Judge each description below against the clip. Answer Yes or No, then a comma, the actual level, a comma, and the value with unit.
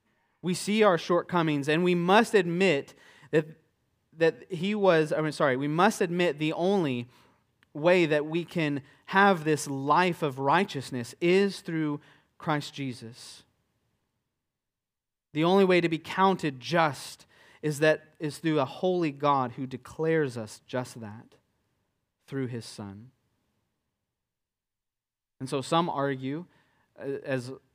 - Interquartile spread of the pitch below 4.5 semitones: No, average, 4.8 semitones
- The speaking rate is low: Yes, slow, 130 wpm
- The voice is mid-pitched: Yes, medium, 150 Hz